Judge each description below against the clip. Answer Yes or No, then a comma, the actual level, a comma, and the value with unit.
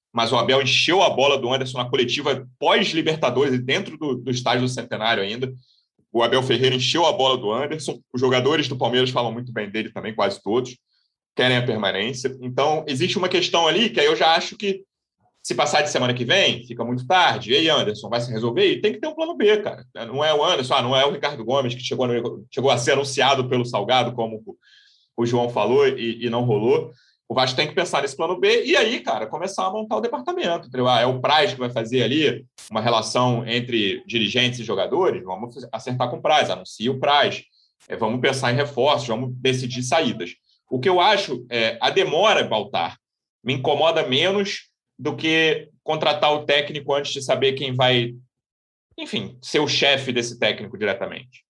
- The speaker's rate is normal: No, fast, 200 wpm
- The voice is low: Yes, low, 130 Hz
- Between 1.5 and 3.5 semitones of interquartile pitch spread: No, average, 4.1 semitones